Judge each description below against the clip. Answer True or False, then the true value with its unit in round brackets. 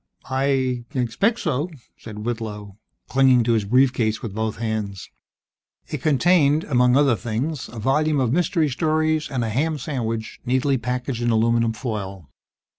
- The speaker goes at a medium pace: True (155 wpm)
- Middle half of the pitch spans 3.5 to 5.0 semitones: True (4.1 semitones)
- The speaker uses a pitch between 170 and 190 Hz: False (125 Hz)